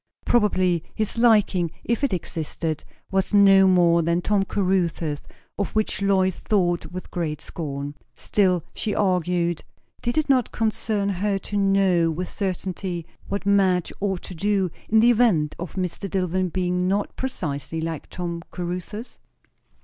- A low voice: No, medium, 185 Hz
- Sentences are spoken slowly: No, average, 145 wpm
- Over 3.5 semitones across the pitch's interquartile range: No, average, 2.8 semitones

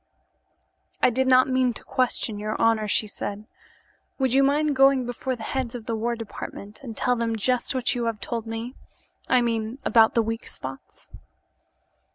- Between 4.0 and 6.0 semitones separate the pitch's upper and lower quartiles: No, narrow, 2.5 semitones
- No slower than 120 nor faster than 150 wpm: No, average, 180 wpm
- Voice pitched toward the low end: No, high, 235 Hz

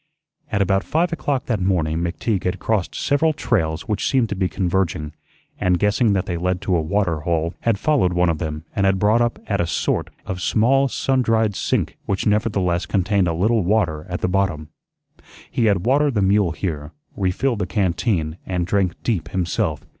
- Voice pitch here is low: Yes, very low, 95 Hz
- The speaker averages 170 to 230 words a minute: Yes, average, 190 wpm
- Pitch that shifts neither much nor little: Yes, average, 4.1 semitones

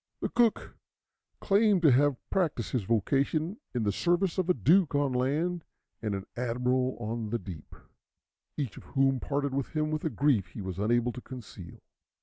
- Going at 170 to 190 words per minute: Yes, average, 175 wpm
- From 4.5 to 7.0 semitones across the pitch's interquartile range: Yes, average, 5.2 semitones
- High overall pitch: No, low, 135 Hz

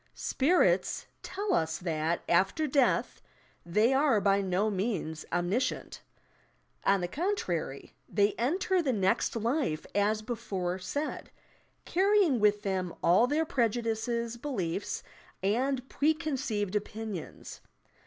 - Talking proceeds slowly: Yes, slow, 115 wpm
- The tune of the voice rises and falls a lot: Yes, wide, 6.4 semitones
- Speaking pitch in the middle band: No, high, 215 Hz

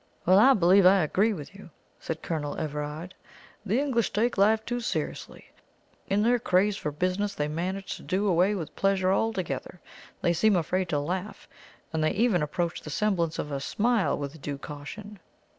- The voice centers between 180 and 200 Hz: Yes, medium, 185 Hz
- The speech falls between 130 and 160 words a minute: No, average, 175 wpm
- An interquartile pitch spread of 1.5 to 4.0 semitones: No, average, 4.8 semitones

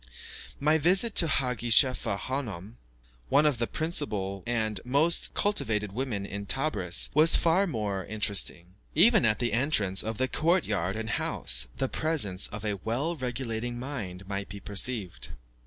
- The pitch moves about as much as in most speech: No, wide, 6.2 semitones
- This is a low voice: Yes, low, 115 Hz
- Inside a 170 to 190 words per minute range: No, average, 155 wpm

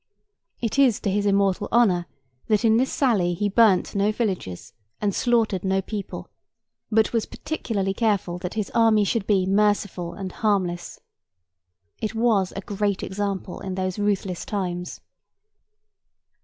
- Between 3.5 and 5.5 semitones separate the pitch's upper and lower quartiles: No, narrow, 2.5 semitones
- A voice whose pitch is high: Yes, high, 200 Hz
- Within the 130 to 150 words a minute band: Yes, average, 140 wpm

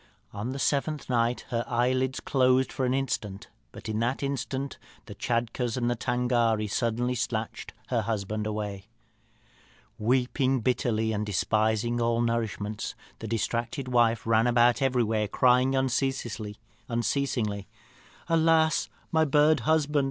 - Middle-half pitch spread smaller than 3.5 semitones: Yes, average, 3.0 semitones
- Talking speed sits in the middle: No, slow, 120 wpm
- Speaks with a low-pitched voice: Yes, low, 120 Hz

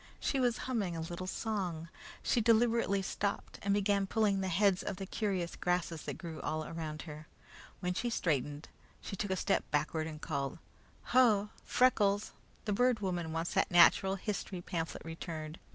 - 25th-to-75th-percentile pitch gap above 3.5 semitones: Yes, average, 4.1 semitones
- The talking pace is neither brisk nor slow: Yes, average, 170 wpm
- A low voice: No, medium, 185 Hz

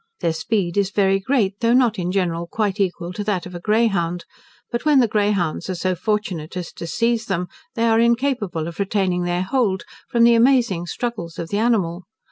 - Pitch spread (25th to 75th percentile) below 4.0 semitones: No, average, 4.6 semitones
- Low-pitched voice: No, high, 195 Hz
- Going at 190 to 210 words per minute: Yes, average, 200 wpm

